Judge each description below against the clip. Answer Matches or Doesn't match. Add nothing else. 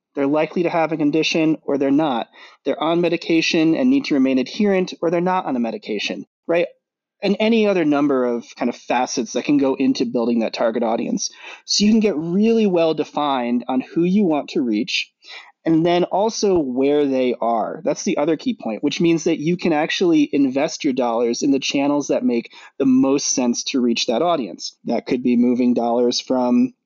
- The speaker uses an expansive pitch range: Matches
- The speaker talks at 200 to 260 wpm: Matches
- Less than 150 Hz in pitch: Doesn't match